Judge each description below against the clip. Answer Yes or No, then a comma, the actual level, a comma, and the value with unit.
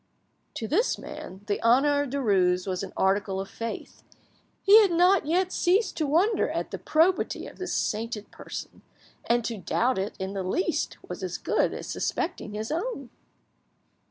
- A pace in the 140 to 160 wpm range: No, average, 170 wpm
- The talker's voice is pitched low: No, high, 245 Hz